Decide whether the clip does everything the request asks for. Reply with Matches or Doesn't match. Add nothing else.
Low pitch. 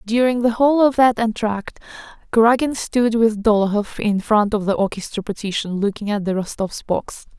Doesn't match